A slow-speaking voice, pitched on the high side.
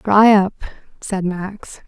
Yes: slow, 130 wpm; high, 195 Hz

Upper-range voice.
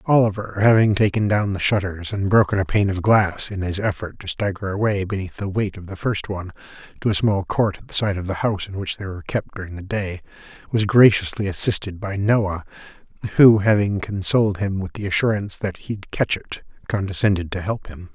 No: low, 100 Hz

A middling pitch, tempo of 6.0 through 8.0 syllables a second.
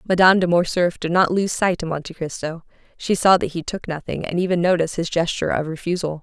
Yes: medium, 175 Hz; 6.3 syllables/s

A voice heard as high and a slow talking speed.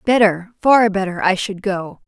Yes: high, 200 Hz; slow, 115 wpm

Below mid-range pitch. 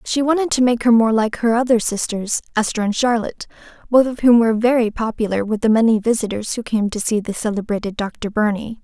No: high, 225 Hz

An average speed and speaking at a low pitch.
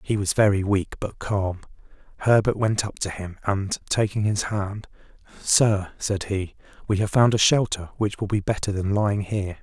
Yes: average, 185 wpm; low, 100 Hz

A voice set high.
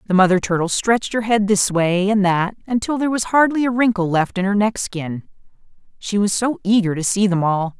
Yes: high, 200 Hz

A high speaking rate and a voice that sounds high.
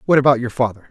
No: fast, 265 wpm; low, 125 Hz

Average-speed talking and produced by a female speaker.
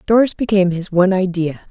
Yes: average, 175 wpm; female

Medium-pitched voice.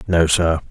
No: very low, 85 Hz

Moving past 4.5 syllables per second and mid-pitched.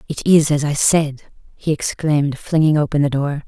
Yes: 5.0 syllables/s; medium, 150 Hz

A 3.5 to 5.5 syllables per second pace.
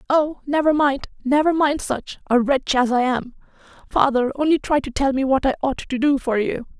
Yes: 5.1 syllables/s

